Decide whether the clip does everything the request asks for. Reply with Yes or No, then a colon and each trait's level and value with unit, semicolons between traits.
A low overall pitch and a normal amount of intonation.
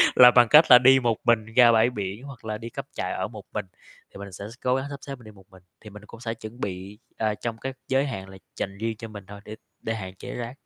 Yes: low, 110 Hz; average, 3.3 semitones